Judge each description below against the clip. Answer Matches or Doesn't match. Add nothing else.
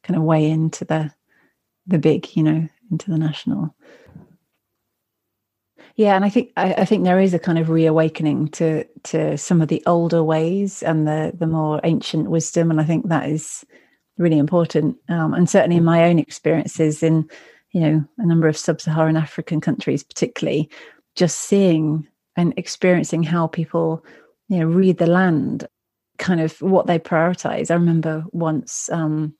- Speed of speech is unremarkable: Matches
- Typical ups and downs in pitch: Doesn't match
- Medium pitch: Matches